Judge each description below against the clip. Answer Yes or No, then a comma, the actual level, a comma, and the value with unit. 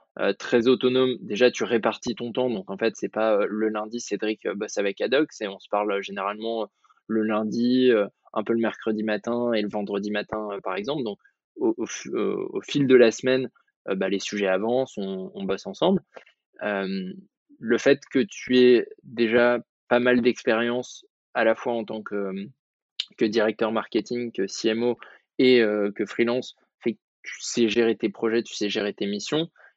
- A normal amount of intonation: Yes, average, 3.1 semitones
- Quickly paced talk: No, average, 200 wpm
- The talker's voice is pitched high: No, low, 115 Hz